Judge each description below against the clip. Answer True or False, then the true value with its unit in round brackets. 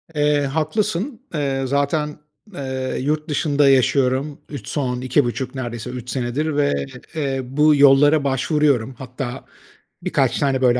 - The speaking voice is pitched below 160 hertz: True (140 Hz)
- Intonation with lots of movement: False (2.4 semitones)